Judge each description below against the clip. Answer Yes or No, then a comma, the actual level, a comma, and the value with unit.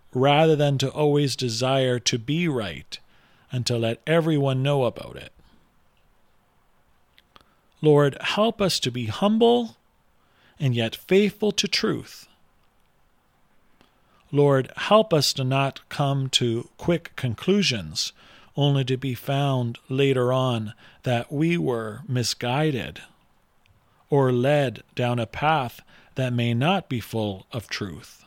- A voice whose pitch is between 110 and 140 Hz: Yes, low, 135 Hz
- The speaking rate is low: Yes, slow, 120 wpm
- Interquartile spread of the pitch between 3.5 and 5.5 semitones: Yes, average, 3.8 semitones